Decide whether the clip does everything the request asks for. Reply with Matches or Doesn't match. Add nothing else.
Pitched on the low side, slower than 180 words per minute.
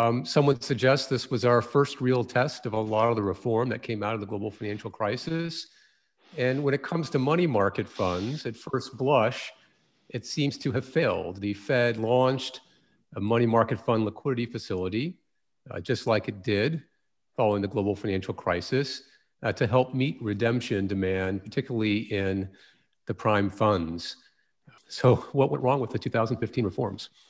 Matches